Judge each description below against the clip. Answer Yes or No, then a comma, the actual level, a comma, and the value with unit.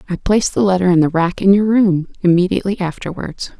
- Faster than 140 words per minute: Yes, average, 200 wpm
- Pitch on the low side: No, medium, 185 Hz